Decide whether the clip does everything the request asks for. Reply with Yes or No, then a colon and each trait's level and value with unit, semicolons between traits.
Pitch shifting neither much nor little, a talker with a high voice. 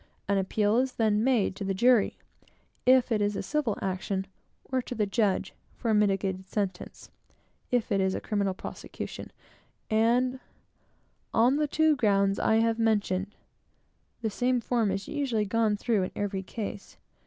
Yes: average, 3.5 semitones; high, 215 Hz